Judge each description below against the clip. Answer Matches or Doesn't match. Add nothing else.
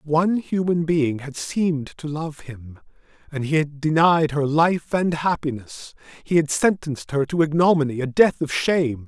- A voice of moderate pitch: Matches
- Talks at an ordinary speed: Matches